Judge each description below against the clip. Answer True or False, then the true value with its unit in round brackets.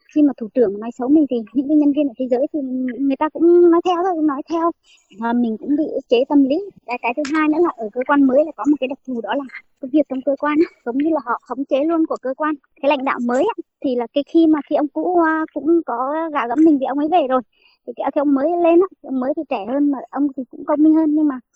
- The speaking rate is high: True (290 wpm)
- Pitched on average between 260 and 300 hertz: True (290 Hz)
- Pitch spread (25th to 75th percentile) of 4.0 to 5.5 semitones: False (3.3 semitones)